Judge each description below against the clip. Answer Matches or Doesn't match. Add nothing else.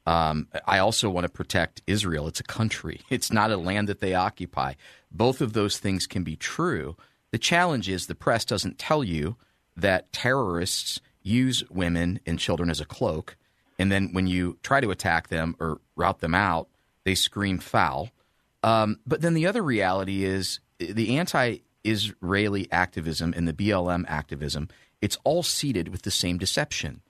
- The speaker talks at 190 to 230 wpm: Doesn't match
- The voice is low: Matches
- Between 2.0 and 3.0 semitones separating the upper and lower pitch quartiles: Doesn't match